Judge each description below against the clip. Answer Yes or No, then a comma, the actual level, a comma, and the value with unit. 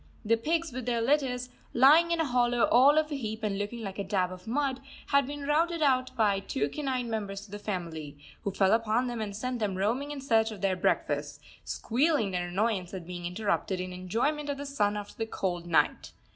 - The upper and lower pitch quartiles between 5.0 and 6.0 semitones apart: Yes, wide, 5.6 semitones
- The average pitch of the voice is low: No, high, 225 Hz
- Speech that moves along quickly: Yes, fast, 220 wpm